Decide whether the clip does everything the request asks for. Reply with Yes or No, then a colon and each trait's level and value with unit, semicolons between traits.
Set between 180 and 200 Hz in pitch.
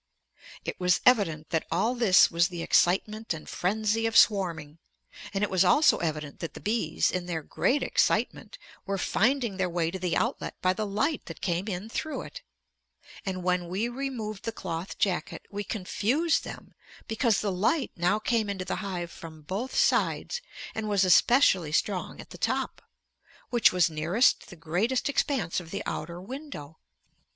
Yes: high, 190 Hz